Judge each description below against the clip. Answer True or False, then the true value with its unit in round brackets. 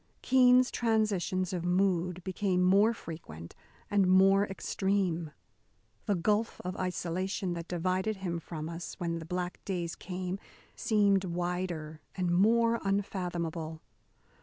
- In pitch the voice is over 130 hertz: True (185 Hz)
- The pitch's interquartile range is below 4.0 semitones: True (2.5 semitones)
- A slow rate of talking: True (120 wpm)